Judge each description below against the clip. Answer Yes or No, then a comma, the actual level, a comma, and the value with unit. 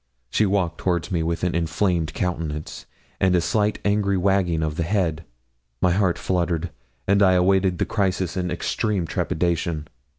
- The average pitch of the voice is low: Yes, very low, 90 Hz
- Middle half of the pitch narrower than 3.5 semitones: Yes, narrow, 2.5 semitones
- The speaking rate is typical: Yes, average, 160 wpm